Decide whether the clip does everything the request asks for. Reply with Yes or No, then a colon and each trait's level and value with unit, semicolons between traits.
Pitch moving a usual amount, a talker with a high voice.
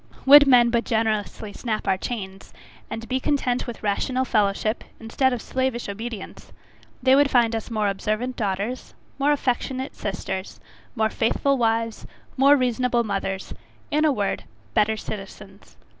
Yes: average, 3.6 semitones; high, 230 Hz